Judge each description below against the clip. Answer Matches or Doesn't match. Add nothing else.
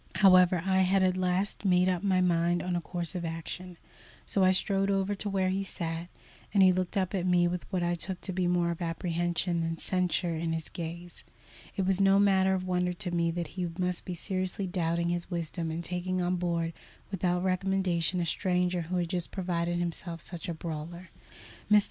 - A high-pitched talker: Doesn't match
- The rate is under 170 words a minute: Doesn't match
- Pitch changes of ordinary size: Doesn't match